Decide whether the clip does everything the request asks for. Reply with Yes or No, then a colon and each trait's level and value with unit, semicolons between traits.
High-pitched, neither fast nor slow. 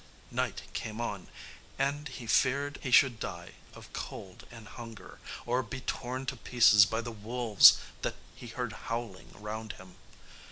No: low, 120 Hz; average, 155 wpm